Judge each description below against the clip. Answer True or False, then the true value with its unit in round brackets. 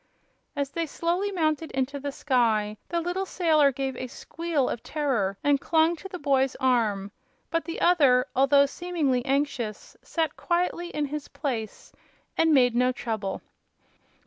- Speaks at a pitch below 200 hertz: False (280 Hz)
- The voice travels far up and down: False (4.6 semitones)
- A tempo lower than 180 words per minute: True (150 wpm)